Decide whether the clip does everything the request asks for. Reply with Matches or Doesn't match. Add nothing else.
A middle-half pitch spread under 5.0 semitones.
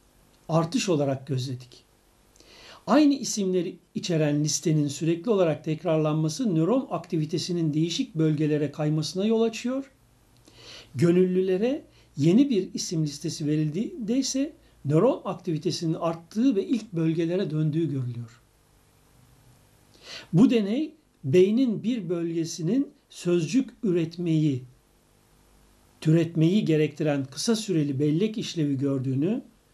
Doesn't match